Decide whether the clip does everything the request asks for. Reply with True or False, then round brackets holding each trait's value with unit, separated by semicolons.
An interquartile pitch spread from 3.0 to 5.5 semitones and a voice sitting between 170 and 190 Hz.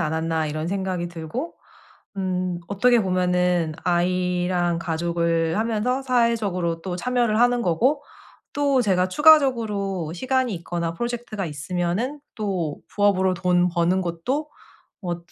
True (5.2 semitones; 185 Hz)